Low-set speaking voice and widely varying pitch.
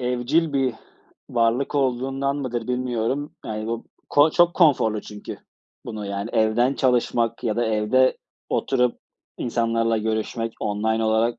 No: low, 120 Hz; average, 2.8 semitones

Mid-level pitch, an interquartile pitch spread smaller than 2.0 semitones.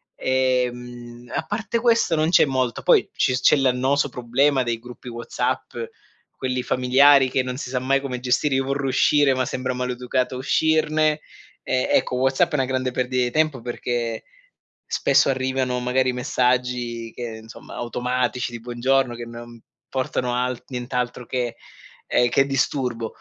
No: low, 125 Hz; narrow, 1.6 semitones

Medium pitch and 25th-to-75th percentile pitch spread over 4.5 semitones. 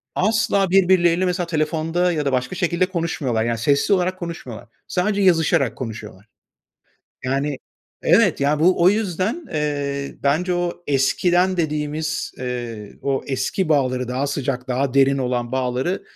Yes: medium, 150 Hz; wide, 5.4 semitones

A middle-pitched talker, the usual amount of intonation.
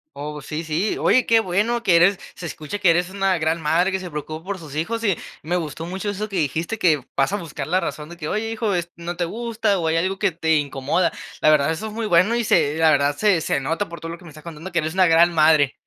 Yes: medium, 170 Hz; average, 3.7 semitones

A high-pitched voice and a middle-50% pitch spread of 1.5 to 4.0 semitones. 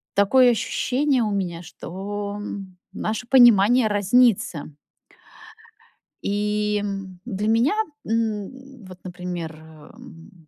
No: high, 205 Hz; average, 4.5 semitones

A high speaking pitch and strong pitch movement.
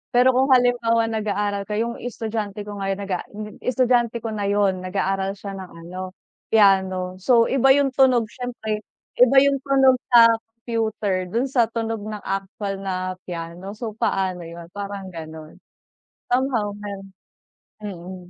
No: high, 210 Hz; average, 3.6 semitones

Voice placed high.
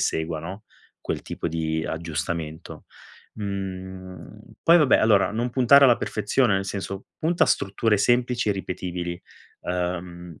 No: very low, 95 Hz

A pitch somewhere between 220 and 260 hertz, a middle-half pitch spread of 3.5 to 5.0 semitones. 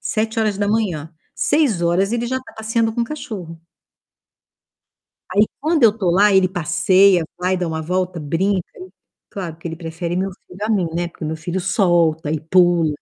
No: medium, 185 Hz; average, 4.0 semitones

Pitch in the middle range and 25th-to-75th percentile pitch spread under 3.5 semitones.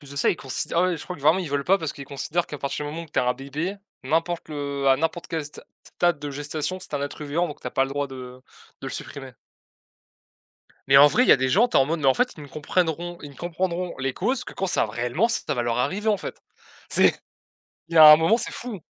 No: medium, 155 Hz; average, 3.9 semitones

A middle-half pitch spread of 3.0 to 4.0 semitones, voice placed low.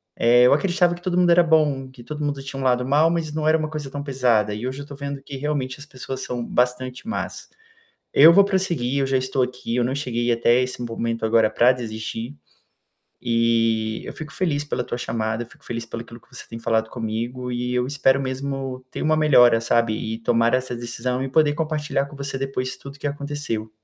Yes: average, 3.6 semitones; low, 130 Hz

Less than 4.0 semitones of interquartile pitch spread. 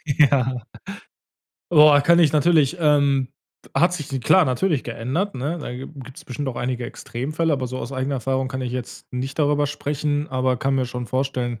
Yes: average, 2.7 semitones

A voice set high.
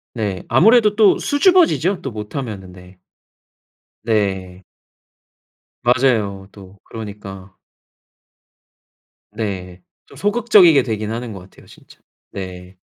No: low, 105 Hz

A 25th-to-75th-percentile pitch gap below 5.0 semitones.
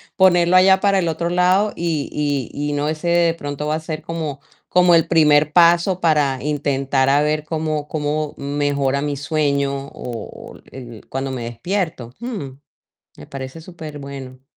Yes: average, 3.4 semitones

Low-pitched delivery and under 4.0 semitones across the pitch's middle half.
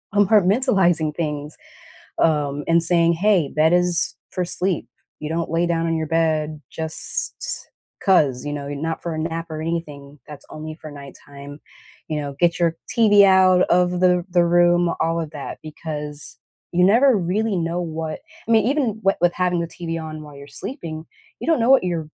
No: medium, 165 Hz; average, 2.7 semitones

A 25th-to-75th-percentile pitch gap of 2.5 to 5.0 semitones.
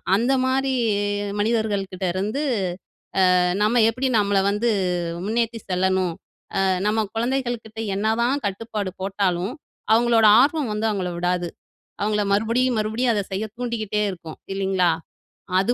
Yes: average, 3.4 semitones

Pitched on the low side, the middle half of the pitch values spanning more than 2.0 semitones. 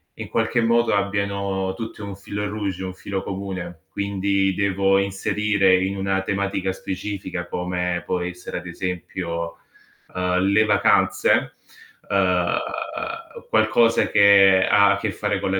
No: very low, 95 Hz; narrow, 1.5 semitones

